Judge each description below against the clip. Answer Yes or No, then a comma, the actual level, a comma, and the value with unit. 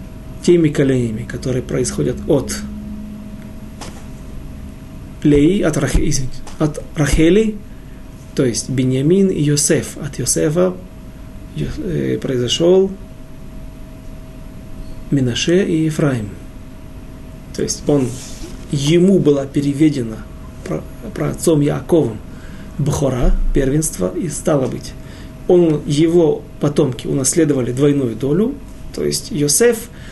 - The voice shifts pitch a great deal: No, average, 4.8 semitones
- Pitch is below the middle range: No, medium, 145 Hz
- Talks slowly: Yes, slow, 90 wpm